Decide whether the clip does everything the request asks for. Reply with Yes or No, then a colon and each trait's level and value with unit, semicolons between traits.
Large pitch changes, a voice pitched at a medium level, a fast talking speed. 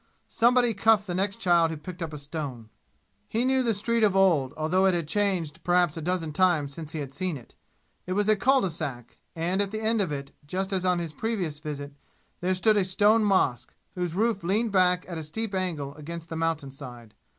No: average, 4.7 semitones; medium, 180 Hz; fast, 220 wpm